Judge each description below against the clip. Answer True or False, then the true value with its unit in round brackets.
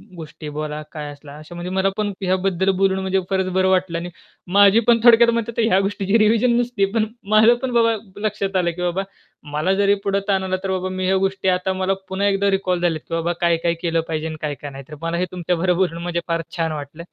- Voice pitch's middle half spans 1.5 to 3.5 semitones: True (2.8 semitones)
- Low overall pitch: False (185 Hz)